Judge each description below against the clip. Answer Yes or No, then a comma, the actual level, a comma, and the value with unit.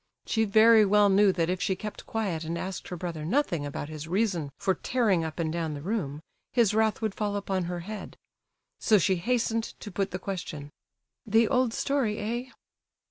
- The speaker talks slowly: No, average, 190 wpm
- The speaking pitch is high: Yes, high, 195 Hz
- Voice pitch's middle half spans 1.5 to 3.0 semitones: No, average, 4.5 semitones